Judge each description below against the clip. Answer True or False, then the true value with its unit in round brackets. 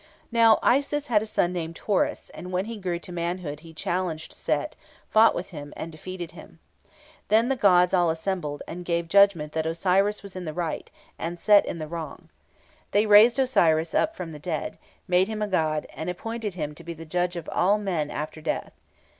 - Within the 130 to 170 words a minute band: False (195 wpm)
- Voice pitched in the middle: True (180 Hz)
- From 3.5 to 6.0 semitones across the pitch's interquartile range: True (4.1 semitones)